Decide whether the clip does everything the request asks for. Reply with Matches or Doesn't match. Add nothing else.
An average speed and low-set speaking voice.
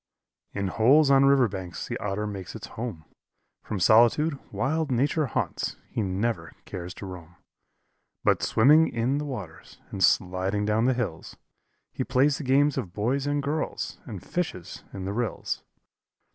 Matches